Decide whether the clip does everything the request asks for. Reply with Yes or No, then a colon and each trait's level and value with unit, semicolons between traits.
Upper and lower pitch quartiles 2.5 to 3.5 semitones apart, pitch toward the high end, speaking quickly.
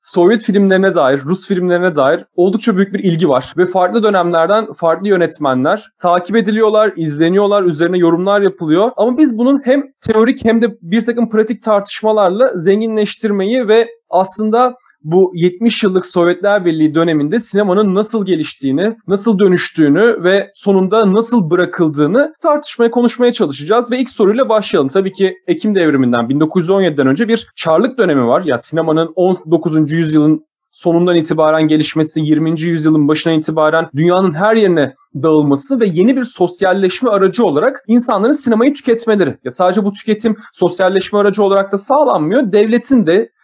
No: average, 4.8 semitones; high, 195 Hz; fast, 145 wpm